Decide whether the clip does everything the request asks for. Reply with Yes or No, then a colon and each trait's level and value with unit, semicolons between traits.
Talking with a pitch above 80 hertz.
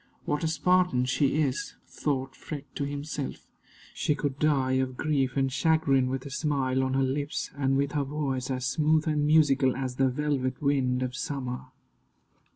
Yes: medium, 140 Hz